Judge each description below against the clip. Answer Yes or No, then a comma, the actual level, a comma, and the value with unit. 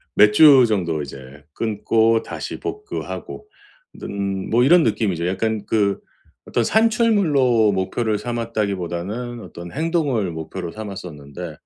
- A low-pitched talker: Yes, low, 110 Hz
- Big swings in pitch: No, average, 4.9 semitones